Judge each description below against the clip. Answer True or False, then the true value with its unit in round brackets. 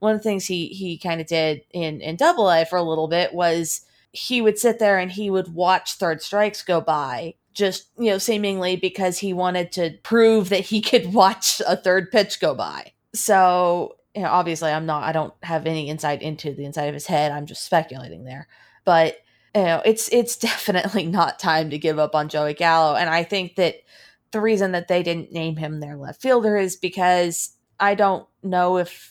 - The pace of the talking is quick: True (210 wpm)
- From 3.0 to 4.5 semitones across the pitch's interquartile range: True (3.6 semitones)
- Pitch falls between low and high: True (180 Hz)